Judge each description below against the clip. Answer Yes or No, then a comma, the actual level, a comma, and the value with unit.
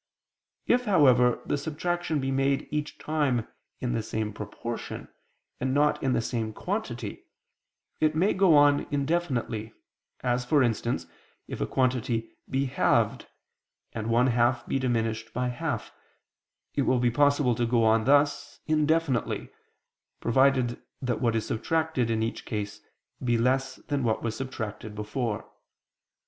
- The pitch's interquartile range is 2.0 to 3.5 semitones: No, average, 3.9 semitones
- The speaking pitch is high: No, low, 125 Hz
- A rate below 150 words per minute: Yes, average, 140 wpm